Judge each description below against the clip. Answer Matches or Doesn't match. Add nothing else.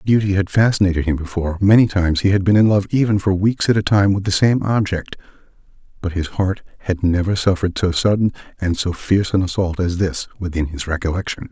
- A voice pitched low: Matches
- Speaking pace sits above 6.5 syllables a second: Doesn't match